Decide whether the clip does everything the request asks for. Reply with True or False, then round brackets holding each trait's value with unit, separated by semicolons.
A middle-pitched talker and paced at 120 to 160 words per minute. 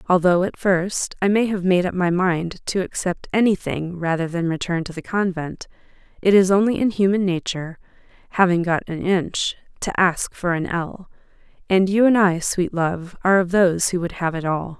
False (180 Hz; 195 wpm)